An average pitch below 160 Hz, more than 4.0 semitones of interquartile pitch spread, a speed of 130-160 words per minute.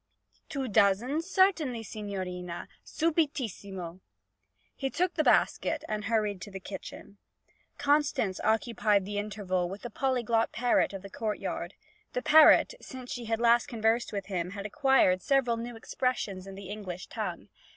No: high, 220 Hz; average, 4.7 semitones; average, 145 wpm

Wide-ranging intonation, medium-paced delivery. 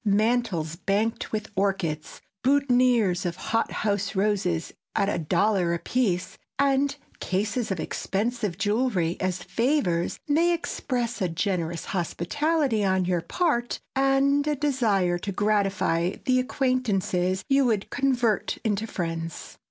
No: wide, 5.7 semitones; slow, 120 wpm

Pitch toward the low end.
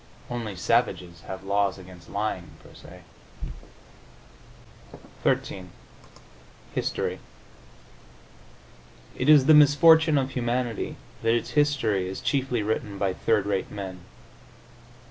Yes: low, 110 Hz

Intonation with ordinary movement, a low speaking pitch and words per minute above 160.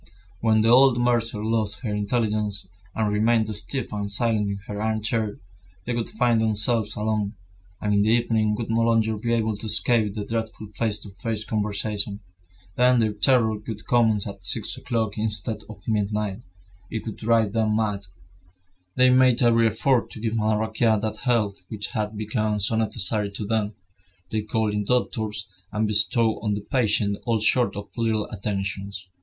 No: narrow, 1.7 semitones; low, 110 Hz; average, 170 wpm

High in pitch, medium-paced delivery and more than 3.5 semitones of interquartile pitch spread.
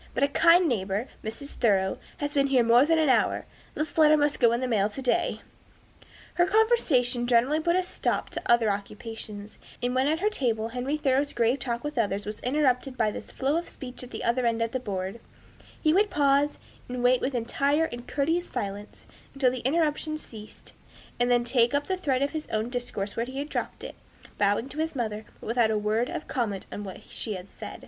No: very high, 250 Hz; fast, 215 wpm; average, 4.4 semitones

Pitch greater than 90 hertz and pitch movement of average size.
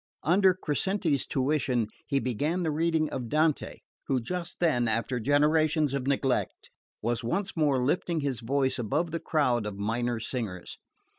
Yes: medium, 140 Hz; average, 4.7 semitones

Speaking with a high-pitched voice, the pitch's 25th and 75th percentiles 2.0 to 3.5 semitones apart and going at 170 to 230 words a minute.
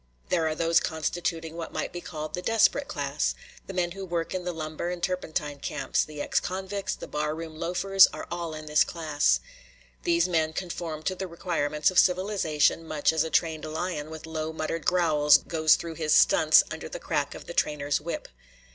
No: medium, 165 Hz; narrow, 2.4 semitones; average, 195 wpm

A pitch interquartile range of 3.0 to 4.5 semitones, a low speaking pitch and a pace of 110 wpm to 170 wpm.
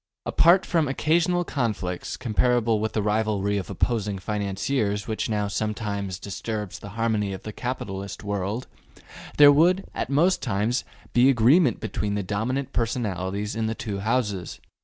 Yes: average, 3.8 semitones; low, 110 Hz; average, 145 wpm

